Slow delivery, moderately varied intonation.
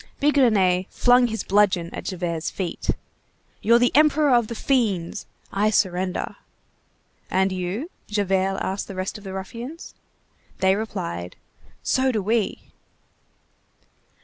Yes: slow, 120 wpm; average, 4.3 semitones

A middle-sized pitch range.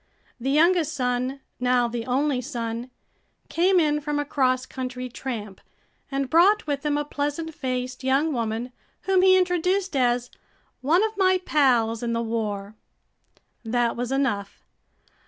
Yes: average, 4.0 semitones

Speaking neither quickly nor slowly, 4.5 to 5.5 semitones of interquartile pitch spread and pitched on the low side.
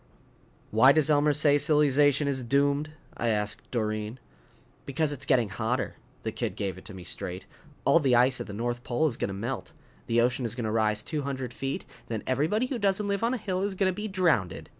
No: fast, 210 wpm; average, 5.1 semitones; low, 130 Hz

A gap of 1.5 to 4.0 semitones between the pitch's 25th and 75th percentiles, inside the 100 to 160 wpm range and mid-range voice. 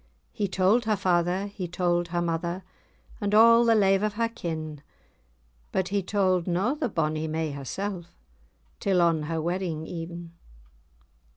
Yes: average, 3.3 semitones; average, 150 wpm; medium, 180 Hz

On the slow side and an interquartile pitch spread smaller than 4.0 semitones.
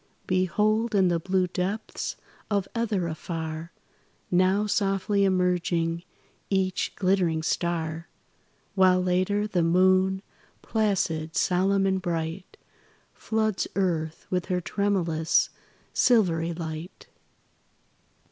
Yes: slow, 95 wpm; average, 2.7 semitones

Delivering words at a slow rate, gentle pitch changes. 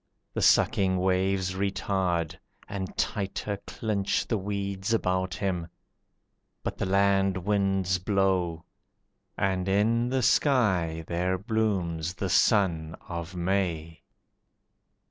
Yes: slow, 105 wpm; narrow, 2.0 semitones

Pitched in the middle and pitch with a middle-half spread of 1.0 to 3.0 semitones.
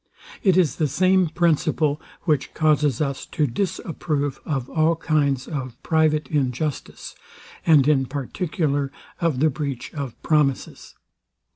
Yes: medium, 150 Hz; narrow, 2.6 semitones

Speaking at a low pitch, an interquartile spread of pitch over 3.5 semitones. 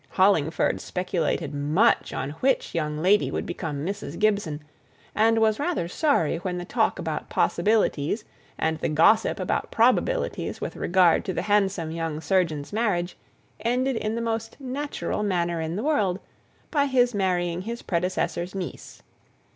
No: high, 190 Hz; average, 5.2 semitones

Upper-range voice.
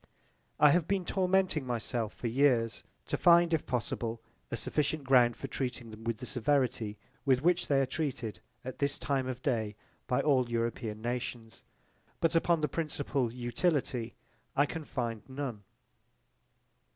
No: low, 130 Hz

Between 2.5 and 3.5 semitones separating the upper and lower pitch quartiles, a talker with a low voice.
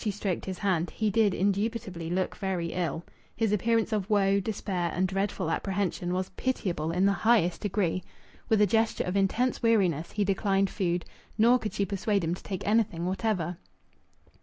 No: average, 2.9 semitones; high, 195 Hz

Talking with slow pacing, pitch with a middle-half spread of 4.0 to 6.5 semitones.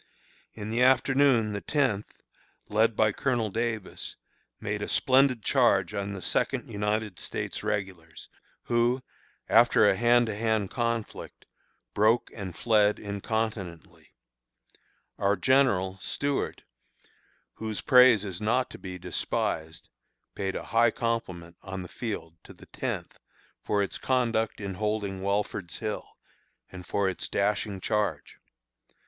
No: slow, 130 wpm; average, 3.3 semitones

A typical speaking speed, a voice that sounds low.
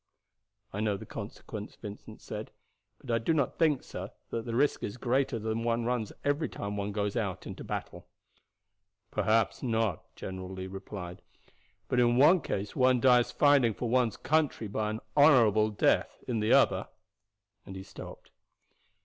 Yes: average, 165 wpm; low, 115 Hz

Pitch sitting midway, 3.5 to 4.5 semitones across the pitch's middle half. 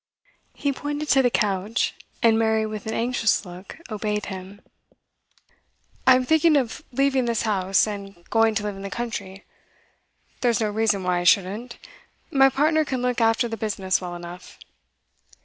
No: high, 220 Hz; average, 4.1 semitones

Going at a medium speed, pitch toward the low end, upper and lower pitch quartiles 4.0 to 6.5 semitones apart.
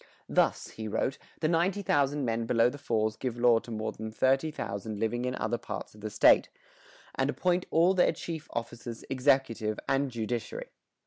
Yes: average, 170 wpm; low, 120 Hz; average, 4.3 semitones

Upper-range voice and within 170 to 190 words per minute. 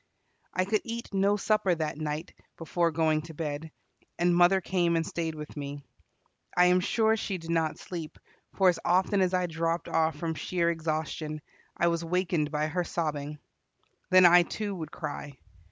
No: medium, 170 Hz; average, 175 wpm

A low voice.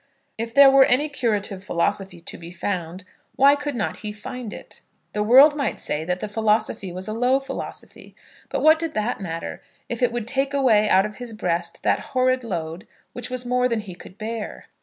No: high, 225 Hz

